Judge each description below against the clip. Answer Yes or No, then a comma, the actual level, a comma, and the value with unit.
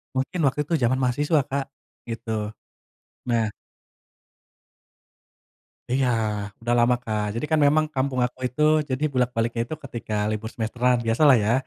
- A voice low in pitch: Yes, low, 125 Hz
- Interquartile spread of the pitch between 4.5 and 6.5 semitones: No, average, 3.3 semitones